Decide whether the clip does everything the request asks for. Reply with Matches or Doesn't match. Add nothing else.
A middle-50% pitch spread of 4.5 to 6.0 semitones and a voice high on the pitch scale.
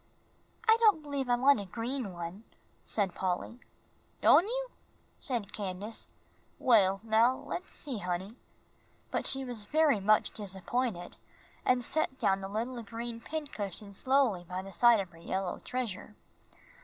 Matches